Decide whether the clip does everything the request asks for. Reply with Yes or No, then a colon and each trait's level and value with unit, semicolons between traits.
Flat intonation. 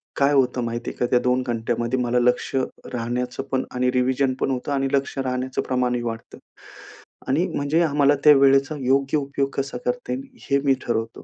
Yes: narrow, 1.9 semitones